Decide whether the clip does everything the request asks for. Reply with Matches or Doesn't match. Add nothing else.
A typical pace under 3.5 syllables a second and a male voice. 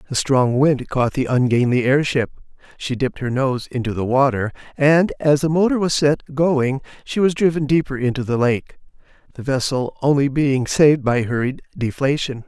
Doesn't match